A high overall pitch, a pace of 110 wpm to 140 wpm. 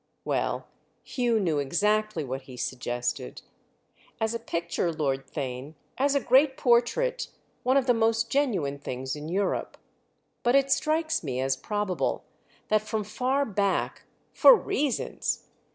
Yes: high, 210 Hz; slow, 135 wpm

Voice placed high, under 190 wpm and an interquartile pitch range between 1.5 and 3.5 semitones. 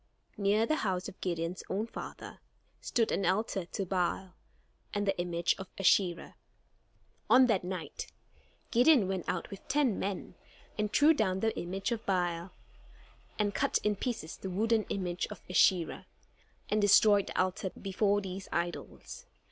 Yes: high, 195 Hz; average, 150 wpm; average, 2.8 semitones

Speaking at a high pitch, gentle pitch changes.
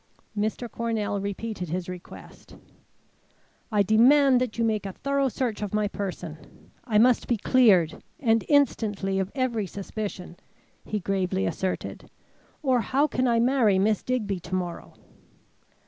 No: high, 215 Hz; average, 4.1 semitones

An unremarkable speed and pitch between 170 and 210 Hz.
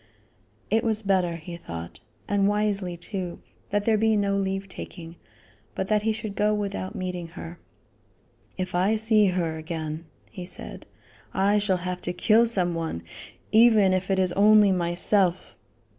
Yes: average, 160 wpm; high, 190 Hz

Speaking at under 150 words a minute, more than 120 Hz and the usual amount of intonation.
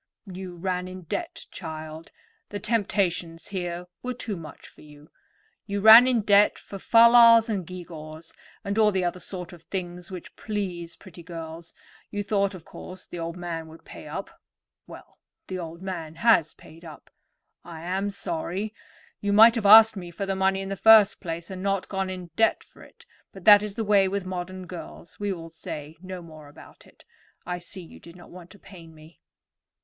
No: average, 195 wpm; medium, 185 Hz; average, 3.2 semitones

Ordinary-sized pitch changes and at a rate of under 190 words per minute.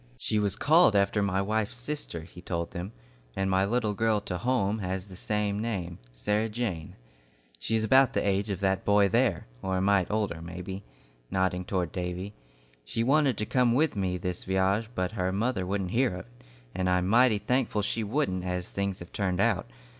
No: average, 3.2 semitones; average, 195 wpm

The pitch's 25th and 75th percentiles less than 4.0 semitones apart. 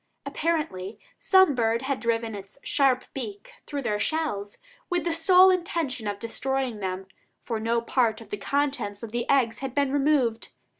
No: average, 4.7 semitones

